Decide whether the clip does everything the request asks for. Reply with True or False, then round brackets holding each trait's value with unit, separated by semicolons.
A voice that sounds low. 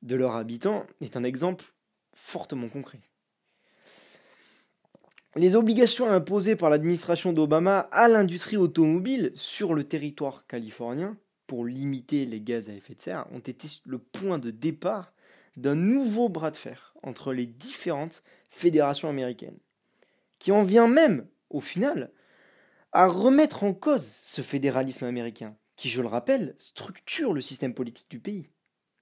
False (155 Hz)